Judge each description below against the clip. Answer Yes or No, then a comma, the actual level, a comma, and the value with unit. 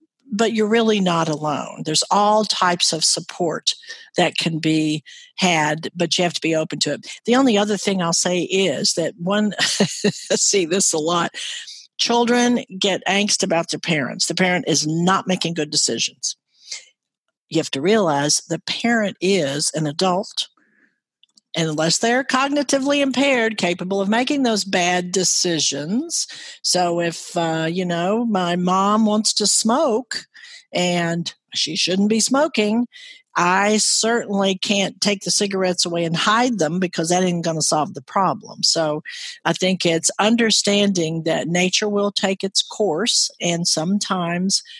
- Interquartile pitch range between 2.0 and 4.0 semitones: No, average, 4.8 semitones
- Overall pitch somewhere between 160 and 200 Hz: Yes, high, 190 Hz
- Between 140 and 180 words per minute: Yes, average, 150 wpm